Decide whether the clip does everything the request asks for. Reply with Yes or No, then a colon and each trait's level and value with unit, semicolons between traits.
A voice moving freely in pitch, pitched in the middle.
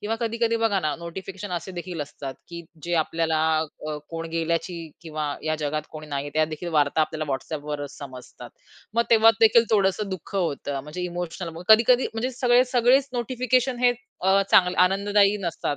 Yes: wide, 5.9 semitones; medium, 180 Hz